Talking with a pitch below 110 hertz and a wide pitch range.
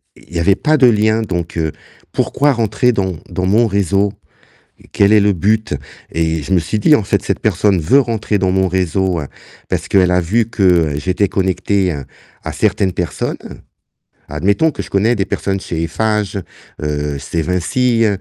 No: very low, 95 Hz; average, 3.7 semitones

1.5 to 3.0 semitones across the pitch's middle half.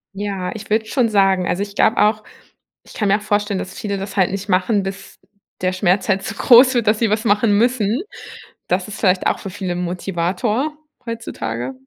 Yes: narrow, 2.5 semitones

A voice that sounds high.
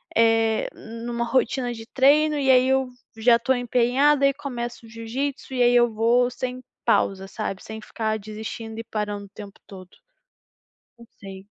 Yes: high, 235 Hz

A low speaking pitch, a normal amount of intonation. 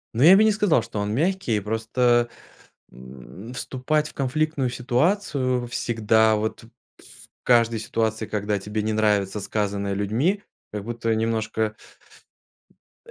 Yes: low, 115 Hz; average, 3.2 semitones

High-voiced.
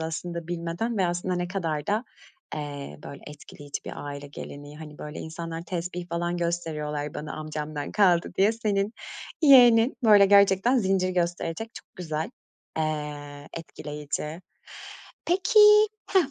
No: medium, 170 Hz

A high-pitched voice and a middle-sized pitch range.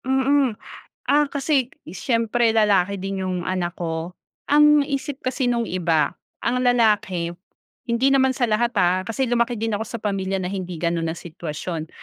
No: high, 215 Hz; wide, 5.8 semitones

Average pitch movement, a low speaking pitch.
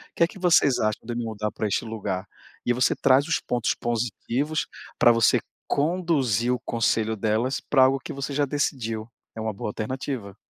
Yes: average, 3.9 semitones; low, 120 Hz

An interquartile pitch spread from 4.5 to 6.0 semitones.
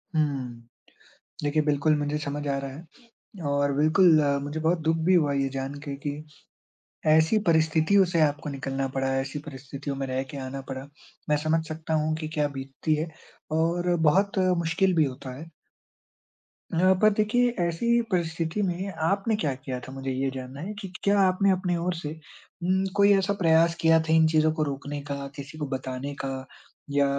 No: average, 3.6 semitones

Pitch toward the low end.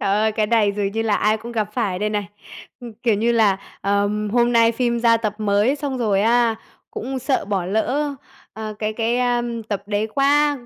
No: high, 220 Hz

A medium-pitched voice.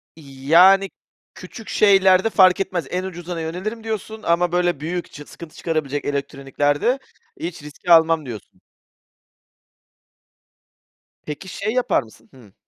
Yes: medium, 170 Hz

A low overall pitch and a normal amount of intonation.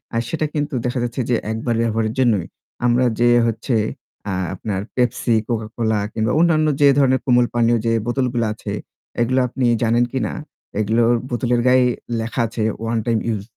No: low, 120 Hz; narrow, 2.0 semitones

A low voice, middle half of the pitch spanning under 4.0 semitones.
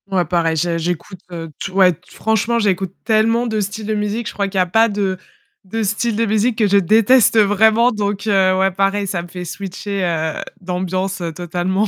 No: high, 195 Hz; average, 3.1 semitones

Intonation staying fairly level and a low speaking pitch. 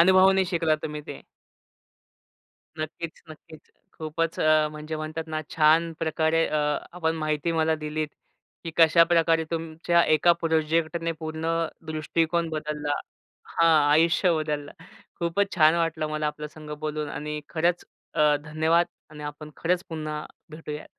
No: narrow, 1.5 semitones; medium, 160 Hz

